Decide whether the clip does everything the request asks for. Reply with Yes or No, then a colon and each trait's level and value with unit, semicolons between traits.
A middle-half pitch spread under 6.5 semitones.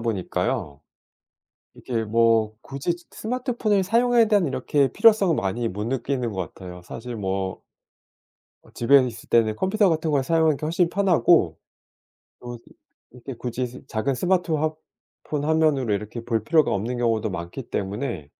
No: wide, 6.8 semitones